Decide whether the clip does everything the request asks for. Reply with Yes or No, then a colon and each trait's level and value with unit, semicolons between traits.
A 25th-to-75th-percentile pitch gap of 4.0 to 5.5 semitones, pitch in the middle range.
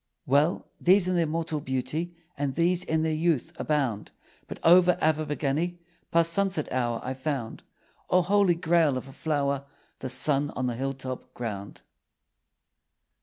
Yes: average, 4.4 semitones; medium, 155 Hz